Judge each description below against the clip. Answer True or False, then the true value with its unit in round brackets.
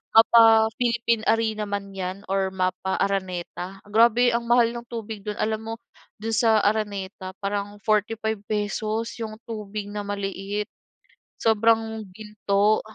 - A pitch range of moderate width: False (2.0 semitones)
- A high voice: True (215 Hz)